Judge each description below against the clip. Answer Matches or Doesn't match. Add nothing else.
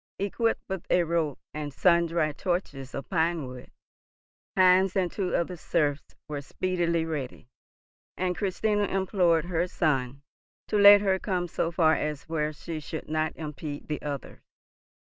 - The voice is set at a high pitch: Doesn't match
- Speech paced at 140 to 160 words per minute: Matches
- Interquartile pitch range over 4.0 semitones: Doesn't match